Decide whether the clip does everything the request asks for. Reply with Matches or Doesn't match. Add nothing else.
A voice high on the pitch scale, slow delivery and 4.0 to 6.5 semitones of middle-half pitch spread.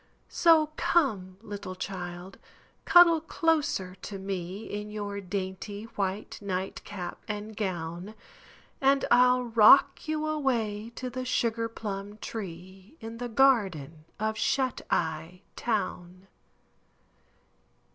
Matches